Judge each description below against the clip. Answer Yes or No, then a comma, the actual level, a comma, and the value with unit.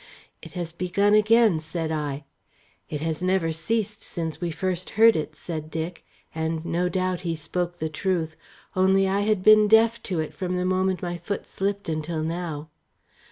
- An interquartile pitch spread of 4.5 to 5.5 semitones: No, average, 3.2 semitones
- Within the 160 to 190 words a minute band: Yes, average, 175 wpm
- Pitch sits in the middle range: Yes, medium, 180 Hz